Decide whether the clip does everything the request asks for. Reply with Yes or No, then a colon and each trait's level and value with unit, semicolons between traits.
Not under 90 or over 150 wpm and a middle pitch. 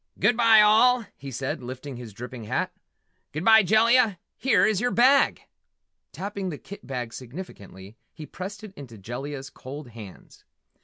Yes: average, 145 wpm; medium, 150 Hz